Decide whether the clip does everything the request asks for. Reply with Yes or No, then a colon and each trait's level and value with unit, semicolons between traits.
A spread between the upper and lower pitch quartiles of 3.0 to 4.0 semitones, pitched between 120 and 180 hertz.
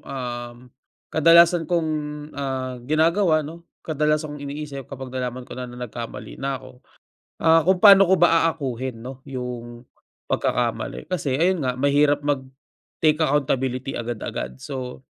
Yes: average, 3.7 semitones; medium, 140 Hz